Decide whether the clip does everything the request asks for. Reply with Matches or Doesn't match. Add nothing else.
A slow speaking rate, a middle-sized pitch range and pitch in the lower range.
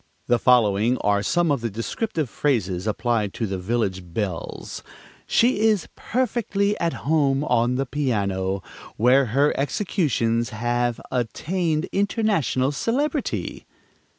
Doesn't match